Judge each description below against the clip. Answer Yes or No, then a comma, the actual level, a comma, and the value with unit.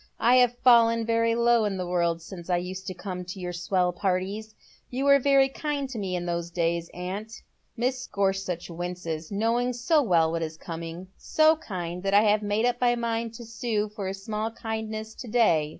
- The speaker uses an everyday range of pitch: Yes, average, 4.7 semitones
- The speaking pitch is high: Yes, high, 205 Hz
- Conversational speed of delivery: No, fast, 215 wpm